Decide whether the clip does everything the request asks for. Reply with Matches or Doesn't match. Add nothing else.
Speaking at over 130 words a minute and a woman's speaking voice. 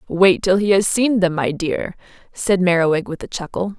Matches